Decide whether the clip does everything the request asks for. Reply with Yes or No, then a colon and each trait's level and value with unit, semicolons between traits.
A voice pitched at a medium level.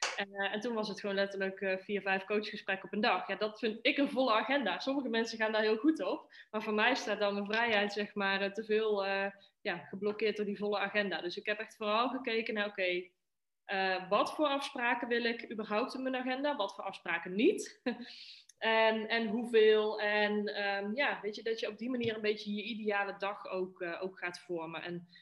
No: high, 210 Hz